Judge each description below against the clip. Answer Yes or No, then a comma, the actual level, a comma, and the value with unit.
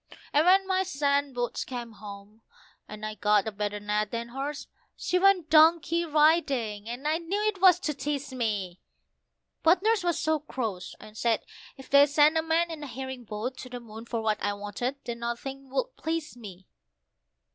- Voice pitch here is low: No, very high, 265 Hz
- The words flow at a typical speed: Yes, average, 190 wpm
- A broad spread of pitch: Yes, wide, 6.6 semitones